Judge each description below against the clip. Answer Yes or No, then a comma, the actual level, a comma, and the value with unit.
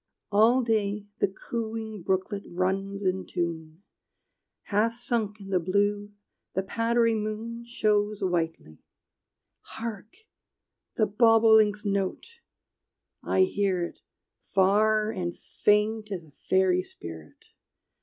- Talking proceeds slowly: Yes, slow, 105 wpm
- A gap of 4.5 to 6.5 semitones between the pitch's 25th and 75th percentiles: No, average, 2.7 semitones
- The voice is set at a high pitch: Yes, high, 205 Hz